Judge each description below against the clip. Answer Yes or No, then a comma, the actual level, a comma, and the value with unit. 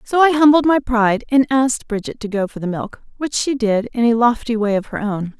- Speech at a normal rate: No, fast, 255 wpm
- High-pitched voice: Yes, high, 235 Hz